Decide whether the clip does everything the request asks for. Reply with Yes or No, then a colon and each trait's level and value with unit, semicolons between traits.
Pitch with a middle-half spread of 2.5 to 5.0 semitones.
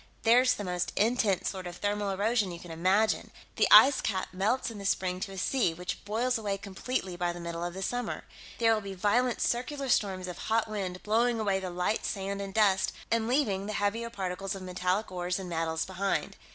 Yes: average, 3.4 semitones